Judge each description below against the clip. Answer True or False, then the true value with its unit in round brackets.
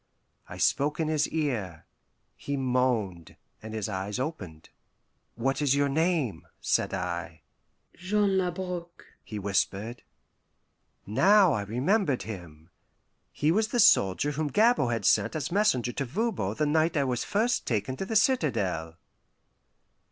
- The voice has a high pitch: False (135 Hz)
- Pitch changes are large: True (9.0 semitones)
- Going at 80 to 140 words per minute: True (135 wpm)